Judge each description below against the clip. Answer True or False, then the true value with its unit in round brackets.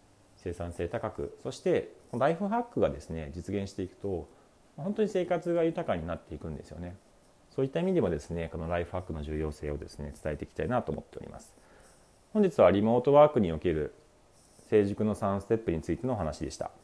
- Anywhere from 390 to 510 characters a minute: False (315 characters per minute)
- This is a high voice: False (95 Hz)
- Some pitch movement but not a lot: False (8.0 semitones)